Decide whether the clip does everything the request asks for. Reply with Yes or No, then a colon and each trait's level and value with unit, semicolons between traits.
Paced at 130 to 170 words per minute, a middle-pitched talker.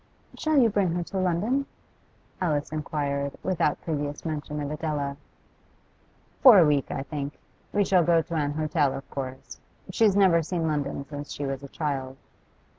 Yes: average, 165 wpm; medium, 155 Hz